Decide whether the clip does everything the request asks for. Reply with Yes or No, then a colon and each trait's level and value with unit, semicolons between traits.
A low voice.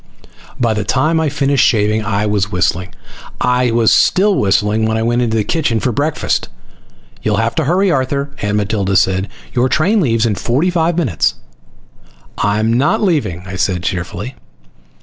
Yes: low, 115 Hz